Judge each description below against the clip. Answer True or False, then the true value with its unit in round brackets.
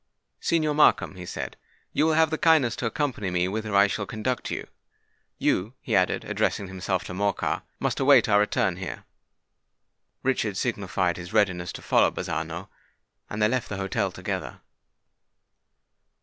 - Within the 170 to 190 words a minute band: False (155 wpm)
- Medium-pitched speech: False (105 Hz)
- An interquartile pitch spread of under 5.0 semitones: False (5.3 semitones)